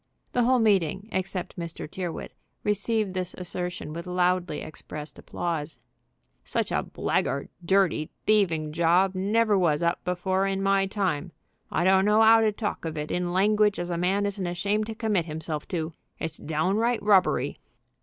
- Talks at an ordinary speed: Yes, average, 160 wpm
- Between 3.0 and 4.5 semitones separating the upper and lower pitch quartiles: Yes, average, 3.3 semitones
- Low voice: No, medium, 185 Hz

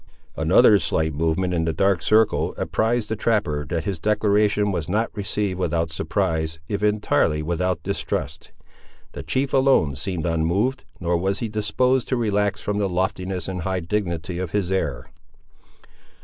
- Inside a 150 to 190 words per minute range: Yes, average, 155 wpm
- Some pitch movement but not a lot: Yes, average, 4.1 semitones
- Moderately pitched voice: No, very low, 95 Hz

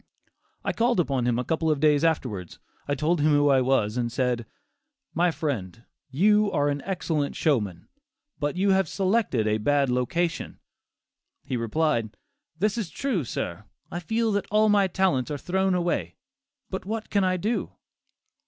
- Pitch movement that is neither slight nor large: No, wide, 7.3 semitones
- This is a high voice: No, medium, 155 Hz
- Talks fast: No, average, 160 wpm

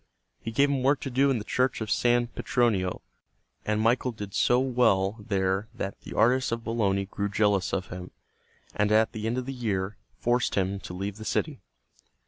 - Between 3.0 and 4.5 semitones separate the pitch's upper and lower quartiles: Yes, average, 3.8 semitones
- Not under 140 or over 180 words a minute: No, average, 195 wpm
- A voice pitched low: Yes, low, 110 Hz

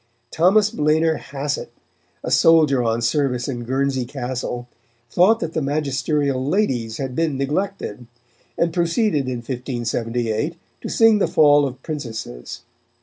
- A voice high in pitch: No, medium, 140 Hz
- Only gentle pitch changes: No, average, 4.7 semitones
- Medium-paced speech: No, slow, 130 wpm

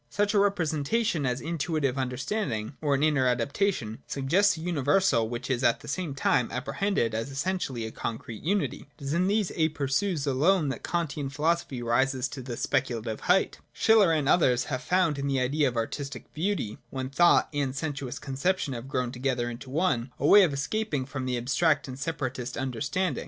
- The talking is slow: No, average, 190 wpm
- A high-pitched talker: No, medium, 140 Hz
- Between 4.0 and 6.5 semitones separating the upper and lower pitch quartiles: Yes, average, 5.0 semitones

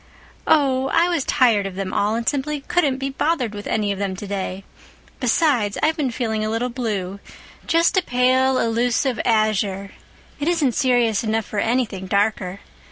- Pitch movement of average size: Yes, average, 4.6 semitones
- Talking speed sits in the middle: Yes, average, 165 wpm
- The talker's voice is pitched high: Yes, high, 230 Hz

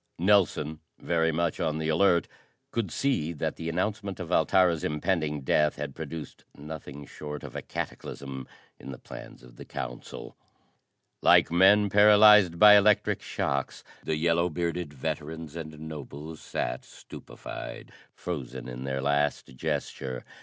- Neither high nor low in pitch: No, very low, 80 Hz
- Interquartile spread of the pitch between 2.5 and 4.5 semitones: Yes, average, 3.6 semitones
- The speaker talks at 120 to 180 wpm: Yes, average, 140 wpm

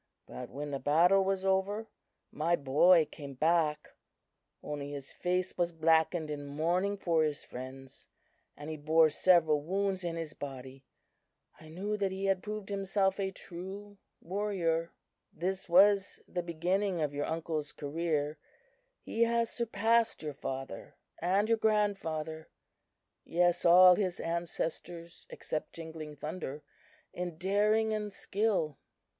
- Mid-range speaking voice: Yes, medium, 170 Hz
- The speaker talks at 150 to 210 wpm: No, slow, 135 wpm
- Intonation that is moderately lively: Yes, average, 4.2 semitones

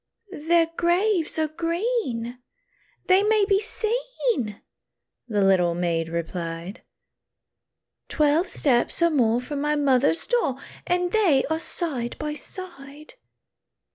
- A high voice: Yes, very high, 300 Hz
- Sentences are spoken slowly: Yes, slow, 110 wpm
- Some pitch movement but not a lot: No, wide, 7.1 semitones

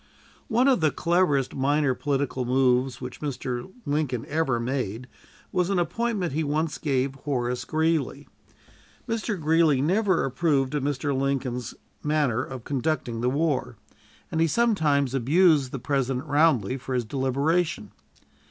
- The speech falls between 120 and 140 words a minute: Yes, slow, 135 wpm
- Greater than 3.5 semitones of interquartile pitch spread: Yes, average, 3.9 semitones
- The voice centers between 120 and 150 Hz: Yes, medium, 140 Hz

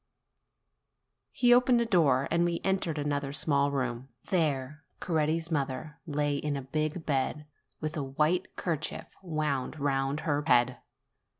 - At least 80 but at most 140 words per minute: Yes, slow, 135 wpm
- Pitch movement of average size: Yes, average, 3.0 semitones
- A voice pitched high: No, medium, 150 Hz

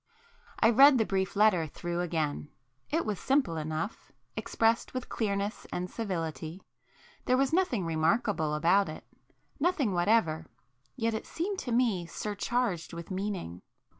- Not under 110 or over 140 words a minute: Yes, slow, 135 wpm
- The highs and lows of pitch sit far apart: Yes, wide, 6.0 semitones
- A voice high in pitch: Yes, high, 200 Hz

